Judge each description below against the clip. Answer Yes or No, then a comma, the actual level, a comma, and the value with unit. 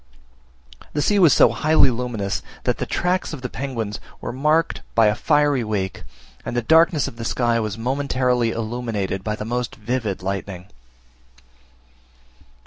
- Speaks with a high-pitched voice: No, low, 120 Hz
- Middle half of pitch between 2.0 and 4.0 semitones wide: No, average, 4.5 semitones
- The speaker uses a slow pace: No, average, 150 wpm